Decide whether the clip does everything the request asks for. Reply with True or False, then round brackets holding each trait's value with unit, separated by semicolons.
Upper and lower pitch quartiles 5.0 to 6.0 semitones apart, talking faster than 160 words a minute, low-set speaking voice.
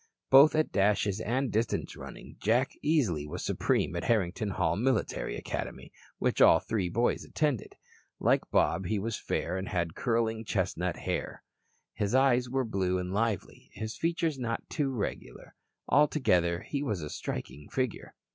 False (5.6 semitones; 155 wpm; 110 Hz)